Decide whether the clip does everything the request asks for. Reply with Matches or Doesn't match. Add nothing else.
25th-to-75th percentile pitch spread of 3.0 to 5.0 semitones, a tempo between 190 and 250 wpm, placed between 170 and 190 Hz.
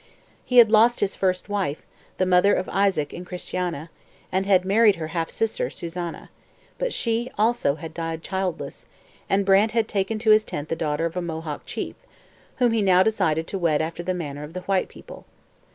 Matches